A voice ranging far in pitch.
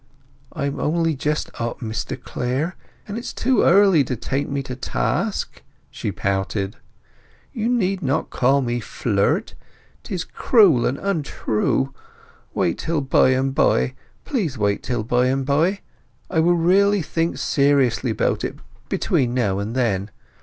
Yes: wide, 5.8 semitones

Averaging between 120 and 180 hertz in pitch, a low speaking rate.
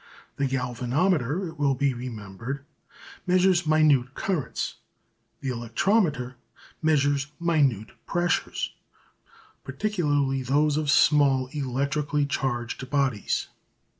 Yes: medium, 140 Hz; slow, 90 wpm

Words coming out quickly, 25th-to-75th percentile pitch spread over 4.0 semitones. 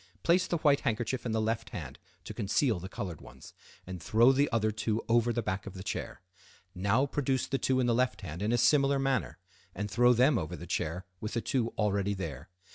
Yes: fast, 220 wpm; average, 4.5 semitones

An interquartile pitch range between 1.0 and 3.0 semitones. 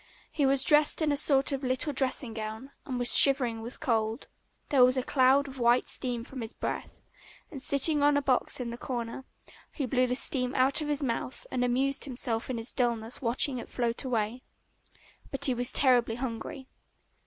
Yes: narrow, 2.5 semitones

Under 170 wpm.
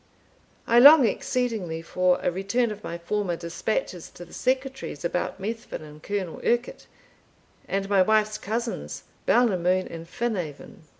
Yes: slow, 135 wpm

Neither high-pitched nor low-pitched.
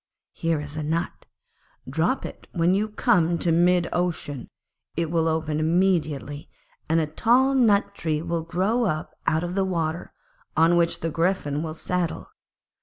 Yes: medium, 165 Hz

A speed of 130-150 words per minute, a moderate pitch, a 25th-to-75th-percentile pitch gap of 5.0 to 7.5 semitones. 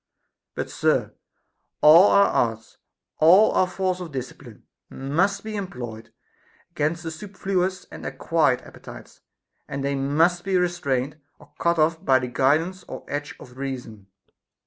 Yes: average, 140 wpm; medium, 155 Hz; average, 5.3 semitones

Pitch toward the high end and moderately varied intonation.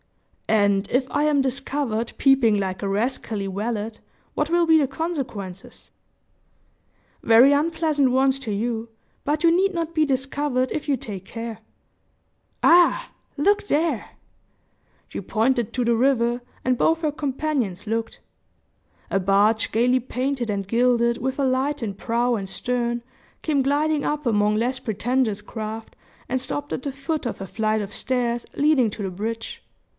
Yes: very high, 250 Hz; average, 4.5 semitones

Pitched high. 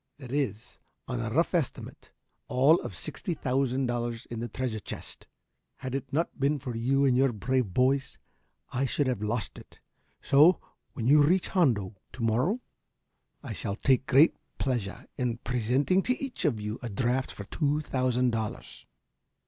No: low, 130 Hz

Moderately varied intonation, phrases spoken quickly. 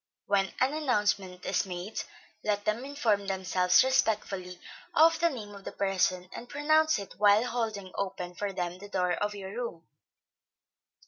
No: average, 4.4 semitones; average, 155 wpm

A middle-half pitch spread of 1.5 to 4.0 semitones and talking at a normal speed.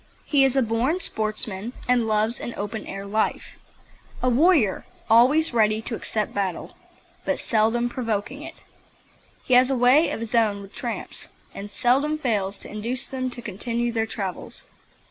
Yes: average, 3.2 semitones; average, 165 wpm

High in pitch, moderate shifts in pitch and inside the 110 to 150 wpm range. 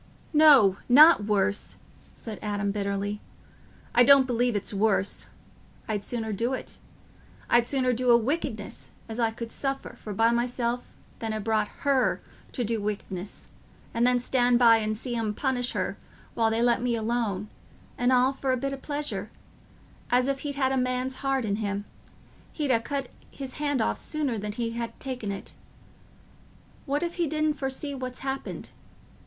No: high, 240 Hz; average, 3.6 semitones; average, 165 wpm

